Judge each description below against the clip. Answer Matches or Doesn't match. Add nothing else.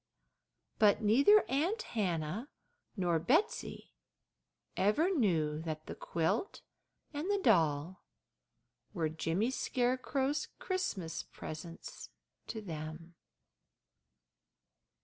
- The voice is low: Doesn't match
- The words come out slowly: Matches